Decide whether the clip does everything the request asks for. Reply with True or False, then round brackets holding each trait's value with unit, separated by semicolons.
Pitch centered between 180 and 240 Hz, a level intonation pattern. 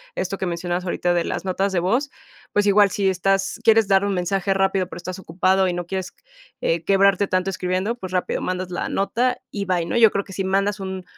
True (190 Hz; 1.5 semitones)